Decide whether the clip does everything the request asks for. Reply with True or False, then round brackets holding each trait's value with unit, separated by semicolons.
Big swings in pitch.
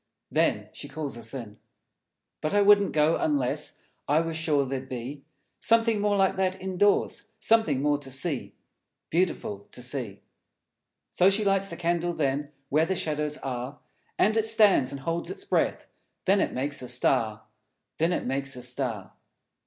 True (6.2 semitones)